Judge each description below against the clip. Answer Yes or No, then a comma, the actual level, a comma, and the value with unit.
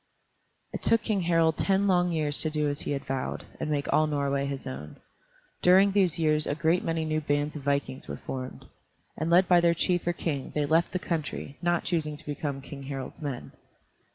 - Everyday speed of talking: No, fast, 210 wpm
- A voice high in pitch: No, medium, 155 Hz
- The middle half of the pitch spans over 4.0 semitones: No, average, 3.3 semitones